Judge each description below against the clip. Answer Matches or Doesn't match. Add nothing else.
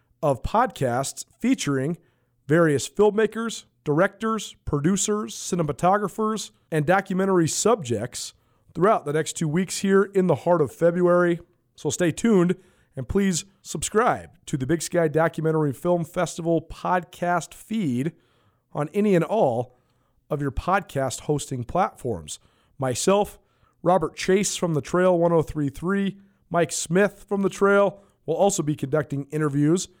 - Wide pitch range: Doesn't match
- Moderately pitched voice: Matches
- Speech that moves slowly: Matches